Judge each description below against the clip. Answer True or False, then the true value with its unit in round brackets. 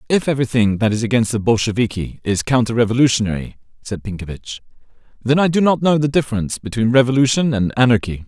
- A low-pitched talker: True (115 Hz)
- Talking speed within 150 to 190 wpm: True (165 wpm)